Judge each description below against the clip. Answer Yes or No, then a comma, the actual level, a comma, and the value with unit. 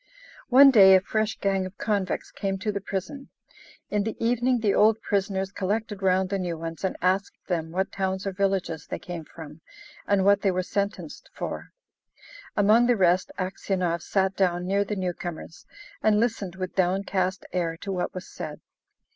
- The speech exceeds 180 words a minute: No, average, 175 wpm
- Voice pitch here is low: No, high, 190 Hz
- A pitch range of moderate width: No, narrow, 1.9 semitones